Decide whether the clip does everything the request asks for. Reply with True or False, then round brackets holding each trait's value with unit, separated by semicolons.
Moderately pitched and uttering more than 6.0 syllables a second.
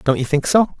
True (160 Hz; 6.8 syllables/s)